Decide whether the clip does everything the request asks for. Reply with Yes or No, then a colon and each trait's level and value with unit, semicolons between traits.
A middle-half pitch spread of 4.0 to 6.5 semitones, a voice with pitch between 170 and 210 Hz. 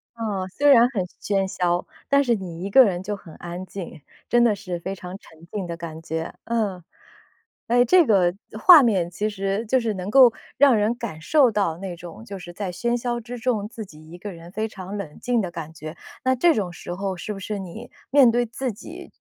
Yes: average, 5.1 semitones; high, 200 Hz